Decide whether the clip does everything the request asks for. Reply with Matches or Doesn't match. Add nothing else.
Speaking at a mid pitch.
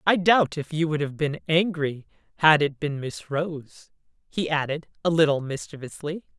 Matches